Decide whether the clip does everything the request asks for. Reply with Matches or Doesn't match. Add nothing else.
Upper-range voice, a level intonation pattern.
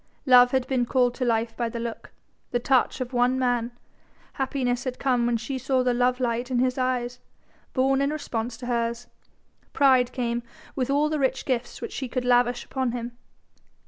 Matches